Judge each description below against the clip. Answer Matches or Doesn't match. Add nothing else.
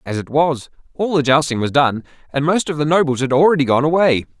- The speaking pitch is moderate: Matches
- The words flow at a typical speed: Doesn't match